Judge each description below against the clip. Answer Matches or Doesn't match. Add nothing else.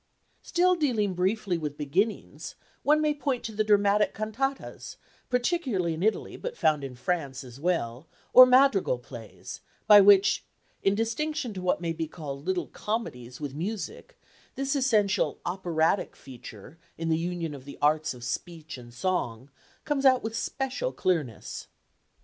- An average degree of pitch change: Doesn't match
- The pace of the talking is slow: Doesn't match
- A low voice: Doesn't match